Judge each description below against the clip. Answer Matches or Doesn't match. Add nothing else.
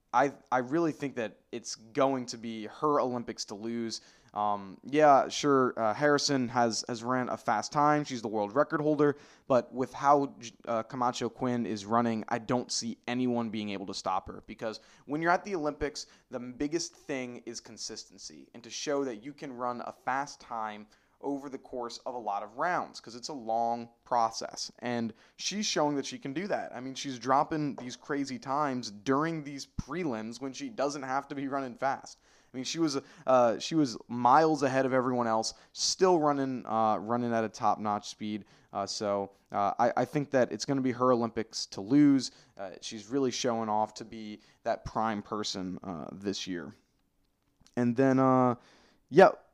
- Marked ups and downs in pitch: Doesn't match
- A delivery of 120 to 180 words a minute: Doesn't match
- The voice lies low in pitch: Matches